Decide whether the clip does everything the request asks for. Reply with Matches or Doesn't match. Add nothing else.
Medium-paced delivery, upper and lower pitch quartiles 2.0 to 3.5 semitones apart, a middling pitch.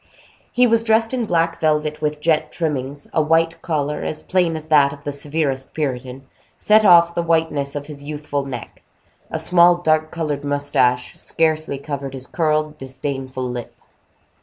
Matches